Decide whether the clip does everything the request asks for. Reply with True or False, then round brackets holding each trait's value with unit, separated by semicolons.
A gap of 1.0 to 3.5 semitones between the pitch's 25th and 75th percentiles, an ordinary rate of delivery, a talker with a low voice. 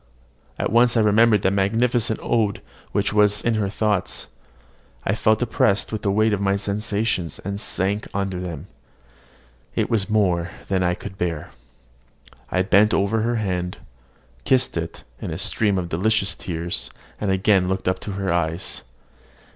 True (2.7 semitones; 160 wpm; 100 Hz)